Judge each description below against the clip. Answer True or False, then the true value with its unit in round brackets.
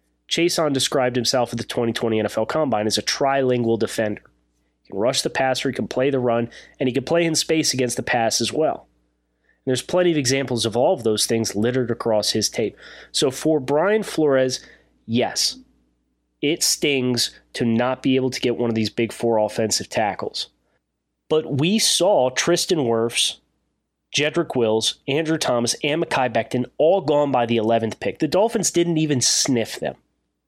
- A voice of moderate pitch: False (125 Hz)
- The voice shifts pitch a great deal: False (4.7 semitones)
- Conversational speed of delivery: True (180 wpm)